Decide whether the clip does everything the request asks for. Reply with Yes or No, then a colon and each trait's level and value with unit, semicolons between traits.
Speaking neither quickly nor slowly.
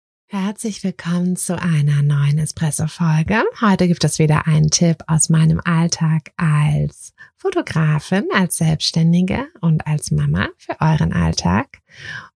No: slow, 120 wpm